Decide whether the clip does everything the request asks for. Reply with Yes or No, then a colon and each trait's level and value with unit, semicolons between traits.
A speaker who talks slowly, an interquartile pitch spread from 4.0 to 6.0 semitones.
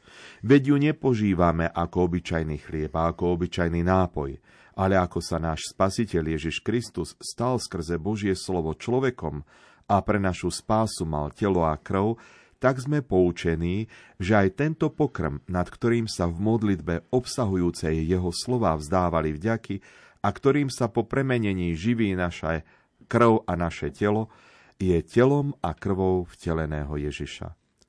No: average, 140 wpm; average, 5.3 semitones